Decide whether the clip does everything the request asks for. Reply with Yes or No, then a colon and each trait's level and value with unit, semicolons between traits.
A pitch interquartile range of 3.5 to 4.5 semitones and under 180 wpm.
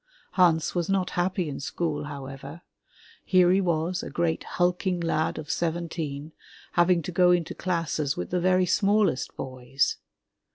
No: average, 3.1 semitones; average, 150 wpm